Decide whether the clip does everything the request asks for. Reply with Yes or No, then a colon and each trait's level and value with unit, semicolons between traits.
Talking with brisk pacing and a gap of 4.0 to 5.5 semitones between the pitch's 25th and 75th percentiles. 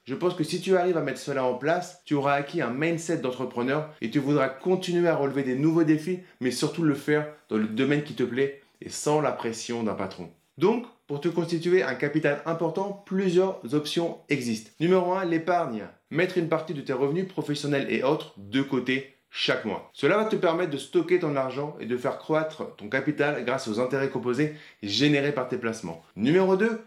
No: average, 205 wpm; average, 4.6 semitones